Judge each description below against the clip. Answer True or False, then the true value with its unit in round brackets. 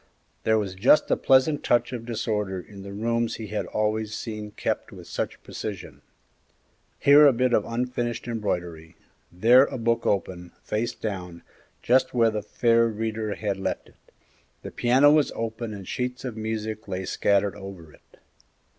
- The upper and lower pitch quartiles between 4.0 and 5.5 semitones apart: False (3.0 semitones)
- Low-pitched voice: True (110 Hz)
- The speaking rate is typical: True (165 wpm)